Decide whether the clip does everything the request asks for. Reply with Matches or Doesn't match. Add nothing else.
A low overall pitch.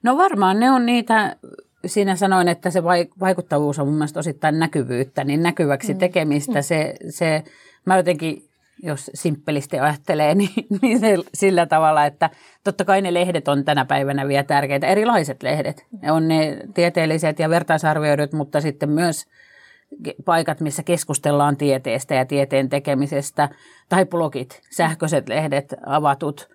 Doesn't match